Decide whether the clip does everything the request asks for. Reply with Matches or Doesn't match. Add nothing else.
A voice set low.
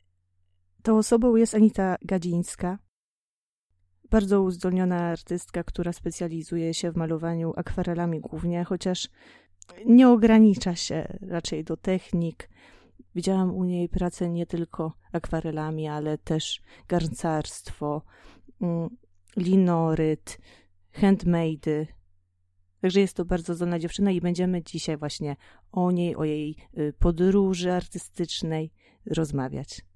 Doesn't match